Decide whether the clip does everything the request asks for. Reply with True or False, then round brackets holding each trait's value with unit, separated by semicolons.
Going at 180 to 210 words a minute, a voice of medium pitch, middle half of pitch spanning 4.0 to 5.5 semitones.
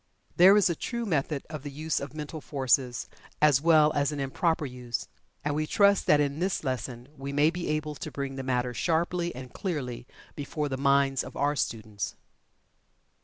False (185 wpm; 145 Hz; 3.0 semitones)